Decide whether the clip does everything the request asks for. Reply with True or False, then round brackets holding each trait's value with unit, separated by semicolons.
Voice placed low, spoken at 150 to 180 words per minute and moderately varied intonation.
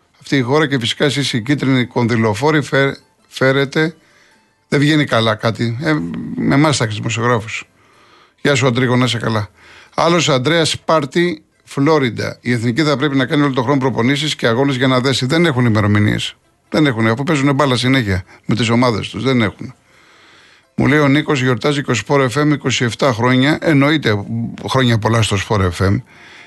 True (130 Hz; 165 wpm; 4.1 semitones)